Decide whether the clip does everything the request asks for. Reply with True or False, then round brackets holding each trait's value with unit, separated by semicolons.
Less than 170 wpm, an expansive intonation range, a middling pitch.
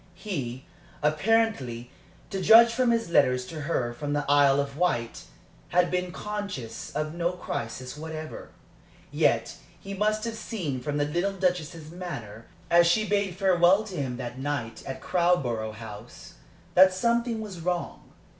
True (150 wpm; 6.6 semitones; 170 Hz)